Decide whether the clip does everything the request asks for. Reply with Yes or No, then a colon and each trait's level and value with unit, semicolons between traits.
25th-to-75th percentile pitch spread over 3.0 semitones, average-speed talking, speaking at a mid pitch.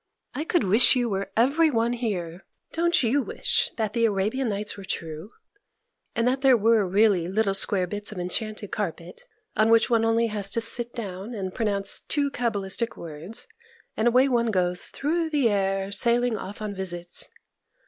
No: average, 3.7 semitones; average, 175 wpm; high, 220 Hz